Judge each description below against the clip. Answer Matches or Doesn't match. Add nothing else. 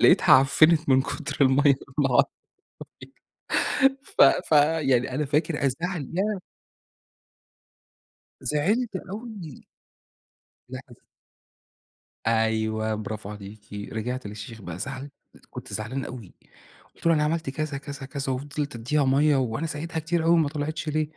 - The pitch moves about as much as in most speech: Matches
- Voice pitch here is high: Doesn't match